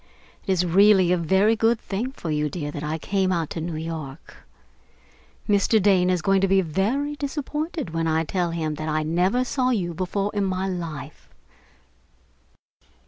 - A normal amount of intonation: Yes, average, 4.0 semitones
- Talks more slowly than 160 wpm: No, average, 175 wpm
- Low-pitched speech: No, medium, 185 Hz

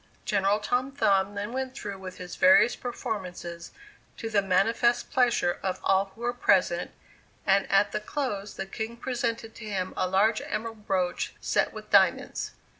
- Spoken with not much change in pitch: No, average, 3.5 semitones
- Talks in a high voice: Yes, high, 205 Hz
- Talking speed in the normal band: Yes, average, 165 wpm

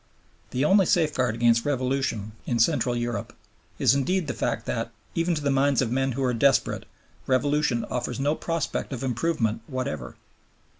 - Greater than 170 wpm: No, average, 160 wpm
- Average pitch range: Yes, average, 3.5 semitones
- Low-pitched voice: Yes, low, 130 Hz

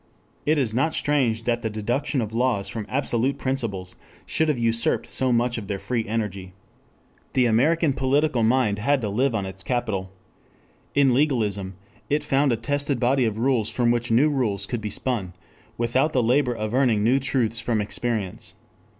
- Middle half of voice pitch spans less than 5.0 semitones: Yes, average, 3.5 semitones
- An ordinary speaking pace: Yes, average, 175 wpm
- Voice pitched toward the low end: Yes, low, 120 Hz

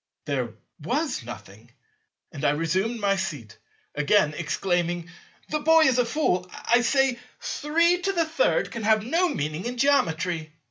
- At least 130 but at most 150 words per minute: Yes, slow, 135 wpm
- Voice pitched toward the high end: Yes, high, 205 Hz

